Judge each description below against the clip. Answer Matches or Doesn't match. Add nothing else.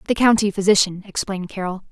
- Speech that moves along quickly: Doesn't match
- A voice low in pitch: Doesn't match